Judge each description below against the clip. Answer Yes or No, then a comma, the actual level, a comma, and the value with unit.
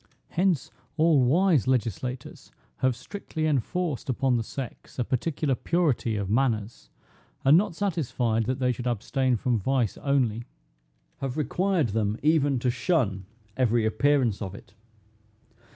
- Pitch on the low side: Yes, low, 130 Hz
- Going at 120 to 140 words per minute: Yes, slow, 135 wpm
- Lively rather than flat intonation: No, average, 4.5 semitones